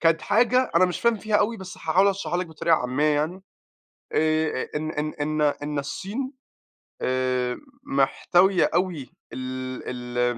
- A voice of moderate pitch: Yes, medium, 155 Hz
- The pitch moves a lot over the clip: Yes, wide, 6.4 semitones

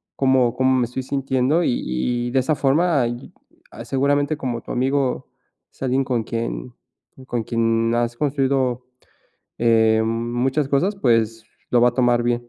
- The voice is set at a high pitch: No, low, 125 Hz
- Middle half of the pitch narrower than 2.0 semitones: No, narrow, 2.4 semitones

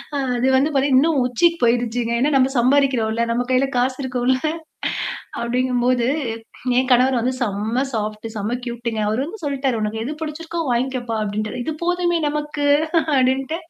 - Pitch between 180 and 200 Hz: No, very high, 255 Hz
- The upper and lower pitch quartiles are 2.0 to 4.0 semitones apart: Yes, average, 2.9 semitones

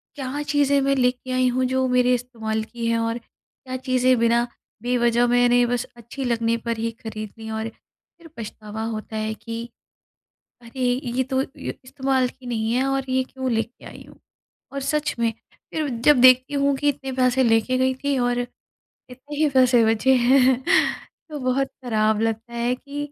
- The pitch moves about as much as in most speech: No, narrow, 2.3 semitones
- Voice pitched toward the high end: Yes, very high, 250 Hz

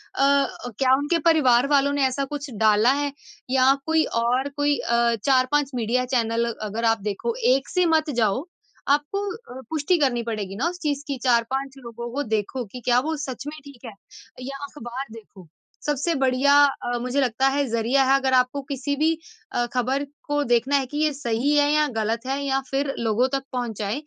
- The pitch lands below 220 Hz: No, very high, 265 Hz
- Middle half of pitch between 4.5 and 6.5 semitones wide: No, average, 3.3 semitones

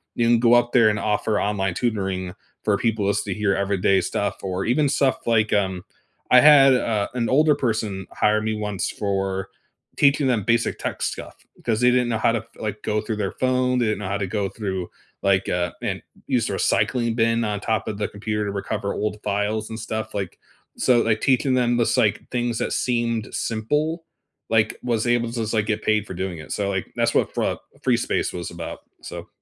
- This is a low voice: Yes, low, 110 Hz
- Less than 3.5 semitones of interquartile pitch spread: Yes, average, 2.9 semitones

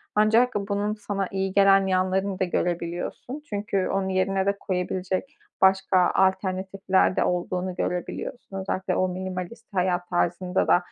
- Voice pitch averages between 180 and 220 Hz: Yes, high, 190 Hz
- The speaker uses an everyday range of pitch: No, narrow, 1.4 semitones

